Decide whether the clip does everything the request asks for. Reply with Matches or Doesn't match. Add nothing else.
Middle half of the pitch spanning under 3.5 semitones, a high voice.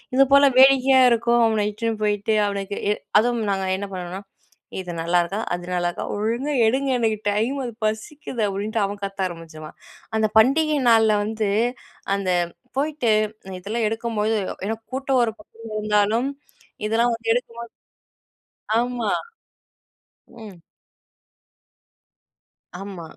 Matches